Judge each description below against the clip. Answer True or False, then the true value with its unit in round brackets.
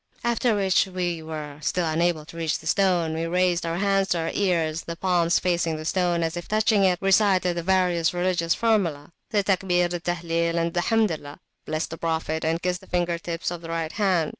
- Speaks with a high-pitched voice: False (175 Hz)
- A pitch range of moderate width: False (2.1 semitones)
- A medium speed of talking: False (215 wpm)